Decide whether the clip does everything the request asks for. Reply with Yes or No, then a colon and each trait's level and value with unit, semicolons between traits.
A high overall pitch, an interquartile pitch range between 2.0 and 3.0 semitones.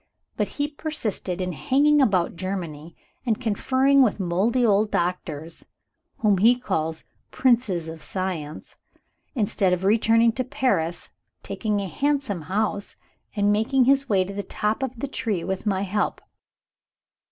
No: high, 205 Hz; wide, 5.5 semitones